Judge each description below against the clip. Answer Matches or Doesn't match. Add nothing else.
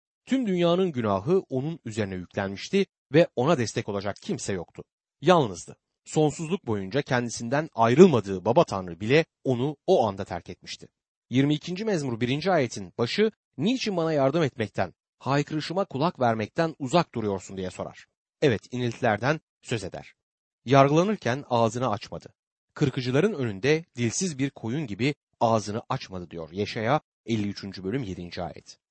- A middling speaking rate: Matches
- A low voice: Matches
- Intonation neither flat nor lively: Doesn't match